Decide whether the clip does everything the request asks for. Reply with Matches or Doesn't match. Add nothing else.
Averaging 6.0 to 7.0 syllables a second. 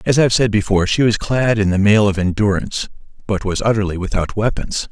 Matches